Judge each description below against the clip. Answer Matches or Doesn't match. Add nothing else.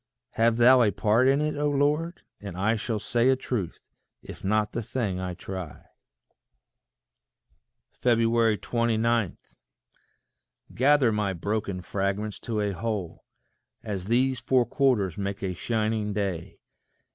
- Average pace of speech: Doesn't match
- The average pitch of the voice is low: Matches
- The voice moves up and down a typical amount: Matches